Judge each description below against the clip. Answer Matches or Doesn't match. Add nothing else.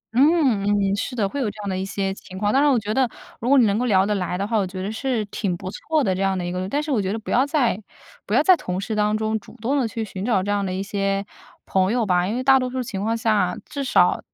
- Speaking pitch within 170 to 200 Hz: Doesn't match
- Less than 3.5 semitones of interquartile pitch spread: Doesn't match